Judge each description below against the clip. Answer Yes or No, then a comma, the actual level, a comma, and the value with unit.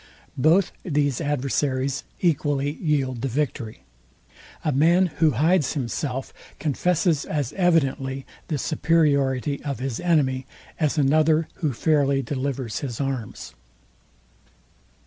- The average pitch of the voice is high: No, medium, 140 Hz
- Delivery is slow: Yes, slow, 110 wpm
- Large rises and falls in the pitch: No, average, 2.8 semitones